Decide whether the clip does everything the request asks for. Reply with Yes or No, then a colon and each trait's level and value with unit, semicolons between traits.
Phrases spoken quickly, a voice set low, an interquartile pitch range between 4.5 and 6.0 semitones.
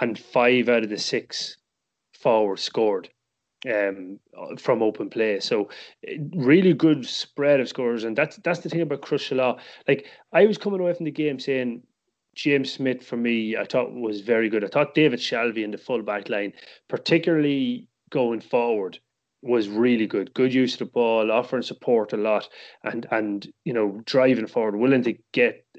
No: average, 180 wpm; low, 125 Hz; average, 5.1 semitones